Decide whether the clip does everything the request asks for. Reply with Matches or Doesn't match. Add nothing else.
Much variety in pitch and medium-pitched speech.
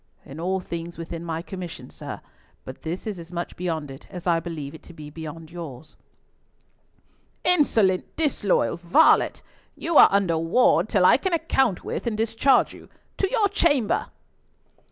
Matches